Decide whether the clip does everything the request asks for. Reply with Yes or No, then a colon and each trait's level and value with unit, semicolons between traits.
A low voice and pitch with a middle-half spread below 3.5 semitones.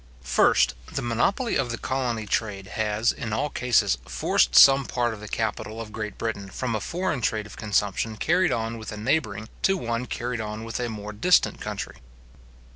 Yes: low, 115 Hz; average, 2.7 semitones